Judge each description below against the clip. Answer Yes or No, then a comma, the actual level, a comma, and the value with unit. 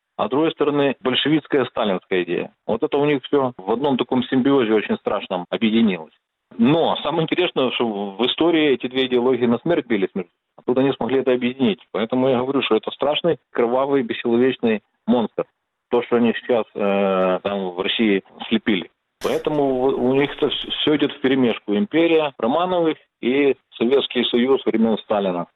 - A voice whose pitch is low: Yes, low, 130 Hz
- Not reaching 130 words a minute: No, fast, 160 wpm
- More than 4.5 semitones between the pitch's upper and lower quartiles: No, average, 3.7 semitones